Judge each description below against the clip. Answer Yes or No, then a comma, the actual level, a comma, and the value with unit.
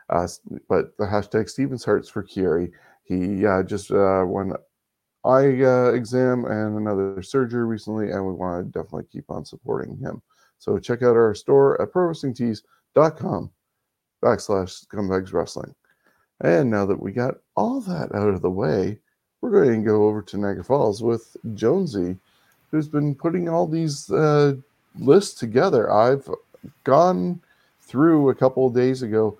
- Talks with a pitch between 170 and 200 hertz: No, low, 120 Hz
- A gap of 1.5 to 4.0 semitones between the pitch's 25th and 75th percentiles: No, average, 5.1 semitones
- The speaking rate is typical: Yes, average, 155 wpm